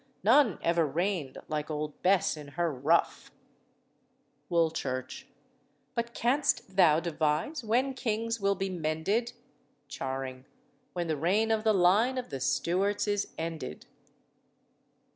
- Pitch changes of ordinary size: No, wide, 5.9 semitones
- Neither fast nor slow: No, slow, 125 wpm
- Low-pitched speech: No, medium, 175 Hz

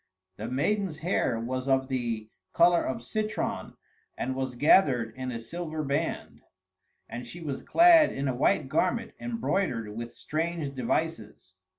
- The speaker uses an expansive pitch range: Yes, wide, 5.8 semitones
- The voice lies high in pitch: No, low, 135 Hz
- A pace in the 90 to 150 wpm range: Yes, average, 145 wpm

